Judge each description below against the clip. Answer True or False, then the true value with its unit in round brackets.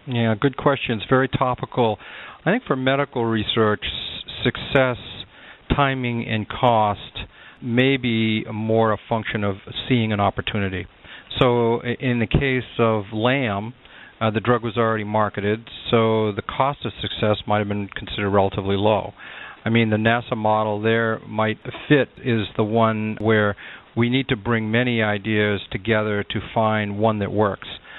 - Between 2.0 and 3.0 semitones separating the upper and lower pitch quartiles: True (2.5 semitones)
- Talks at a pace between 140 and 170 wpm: True (150 wpm)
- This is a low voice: True (110 Hz)